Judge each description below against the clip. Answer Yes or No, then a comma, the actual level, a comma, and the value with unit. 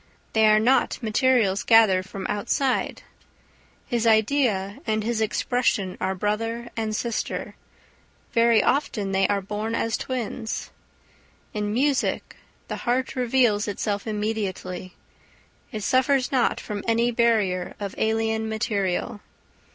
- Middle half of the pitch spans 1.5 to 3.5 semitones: Yes, narrow, 2.6 semitones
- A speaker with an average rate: No, slow, 120 wpm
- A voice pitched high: Yes, high, 220 Hz